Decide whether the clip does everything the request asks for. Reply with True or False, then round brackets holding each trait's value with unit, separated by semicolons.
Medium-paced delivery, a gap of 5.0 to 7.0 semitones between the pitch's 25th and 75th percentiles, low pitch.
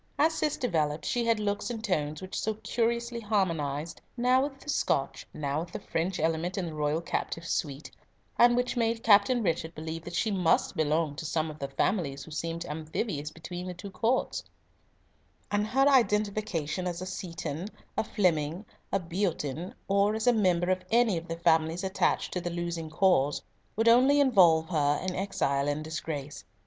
False (180 wpm; 5.3 semitones; 180 Hz)